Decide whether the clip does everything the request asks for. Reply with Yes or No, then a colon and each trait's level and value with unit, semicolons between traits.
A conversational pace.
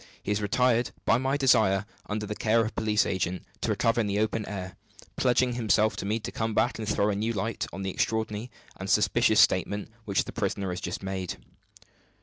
No: fast, 210 wpm